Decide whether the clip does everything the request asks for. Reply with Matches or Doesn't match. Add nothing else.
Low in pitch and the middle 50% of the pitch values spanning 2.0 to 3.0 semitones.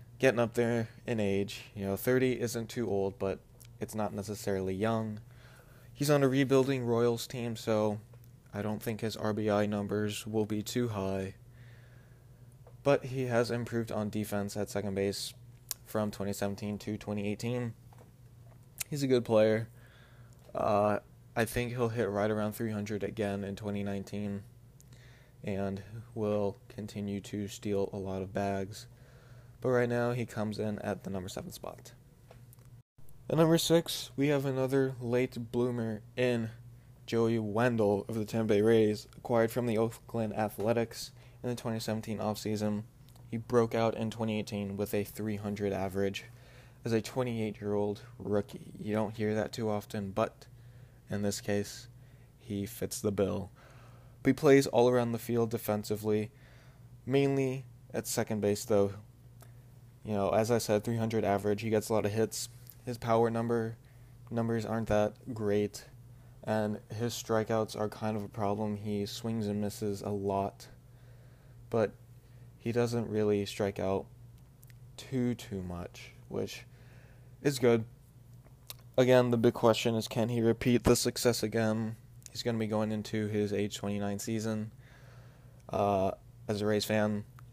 Matches